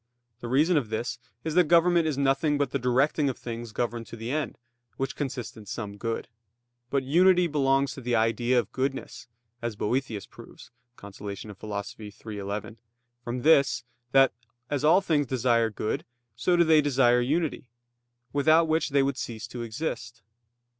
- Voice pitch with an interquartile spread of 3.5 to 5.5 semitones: Yes, average, 4.4 semitones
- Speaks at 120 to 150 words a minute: No, average, 170 wpm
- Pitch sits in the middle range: No, low, 130 Hz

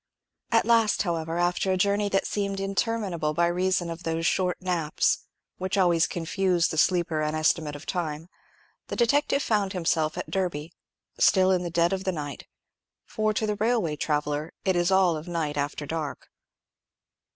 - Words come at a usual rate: Yes, average, 165 wpm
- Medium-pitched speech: Yes, medium, 175 Hz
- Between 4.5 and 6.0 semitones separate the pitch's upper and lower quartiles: No, average, 3.3 semitones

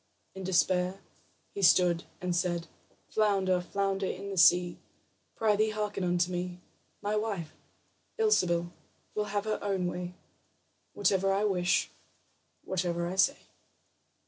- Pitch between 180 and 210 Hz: Yes, medium, 185 Hz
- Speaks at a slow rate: Yes, slow, 120 wpm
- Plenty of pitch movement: No, narrow, 2.4 semitones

